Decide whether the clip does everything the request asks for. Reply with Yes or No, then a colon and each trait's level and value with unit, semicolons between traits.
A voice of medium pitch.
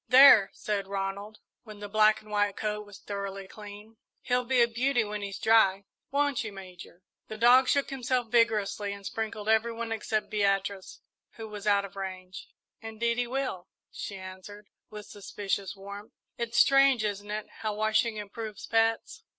No: high, 210 Hz